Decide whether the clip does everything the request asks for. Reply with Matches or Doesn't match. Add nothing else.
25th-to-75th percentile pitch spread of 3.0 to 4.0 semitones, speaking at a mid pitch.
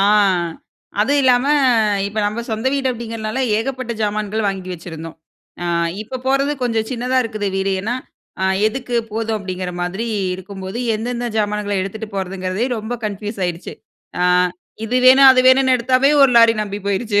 Doesn't match